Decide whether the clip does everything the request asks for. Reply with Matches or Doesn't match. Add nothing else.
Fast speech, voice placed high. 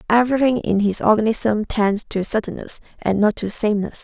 Doesn't match